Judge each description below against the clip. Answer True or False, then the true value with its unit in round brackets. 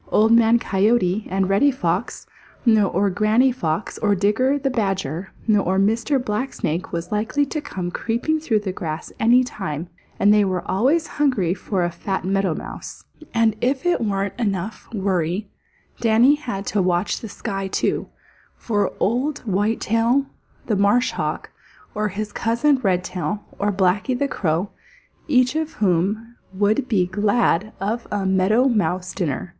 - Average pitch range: True (3.9 semitones)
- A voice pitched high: True (210 Hz)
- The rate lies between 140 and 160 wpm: True (150 wpm)